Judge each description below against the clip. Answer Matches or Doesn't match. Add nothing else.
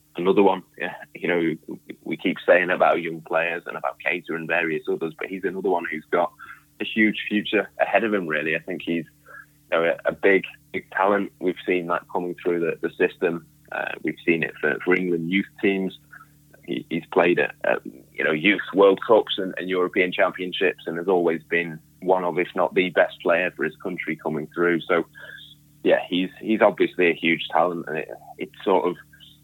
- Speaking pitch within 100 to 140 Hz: Doesn't match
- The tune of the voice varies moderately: Doesn't match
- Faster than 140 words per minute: Matches